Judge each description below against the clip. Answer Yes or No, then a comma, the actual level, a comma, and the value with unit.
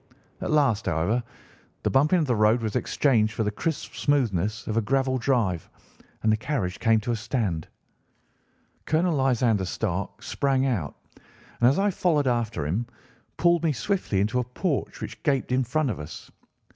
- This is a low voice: Yes, low, 120 Hz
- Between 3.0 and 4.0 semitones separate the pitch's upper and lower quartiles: No, average, 4.8 semitones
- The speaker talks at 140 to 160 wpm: No, average, 170 wpm